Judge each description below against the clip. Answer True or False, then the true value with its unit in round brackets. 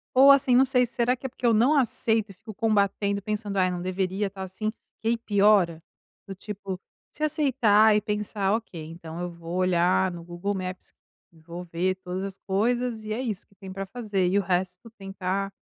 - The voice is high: True (200 Hz)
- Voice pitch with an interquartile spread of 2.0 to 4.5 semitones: True (3.3 semitones)